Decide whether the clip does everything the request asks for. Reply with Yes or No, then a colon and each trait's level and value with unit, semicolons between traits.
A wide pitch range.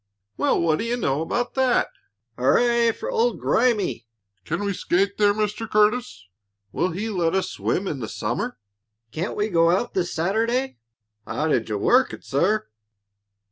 Yes: wide, 6.2 semitones